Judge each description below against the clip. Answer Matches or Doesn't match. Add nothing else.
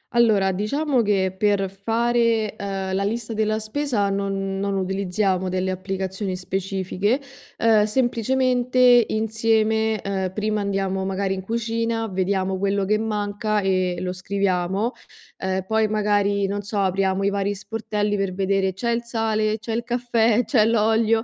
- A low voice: Doesn't match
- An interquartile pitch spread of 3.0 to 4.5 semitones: Doesn't match